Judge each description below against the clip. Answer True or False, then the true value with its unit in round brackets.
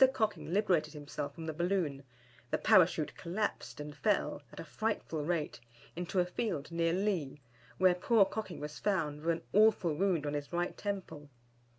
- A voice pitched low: False (170 Hz)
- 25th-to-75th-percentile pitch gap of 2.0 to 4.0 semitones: False (4.8 semitones)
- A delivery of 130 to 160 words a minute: False (170 wpm)